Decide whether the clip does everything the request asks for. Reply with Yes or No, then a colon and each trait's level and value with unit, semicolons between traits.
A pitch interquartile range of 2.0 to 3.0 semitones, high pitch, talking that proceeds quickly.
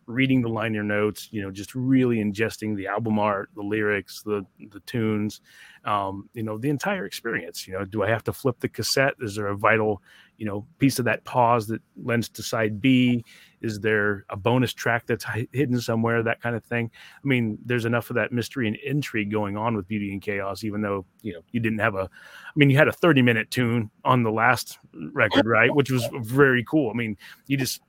No: average, 2.7 semitones; low, 115 Hz; fast, 220 wpm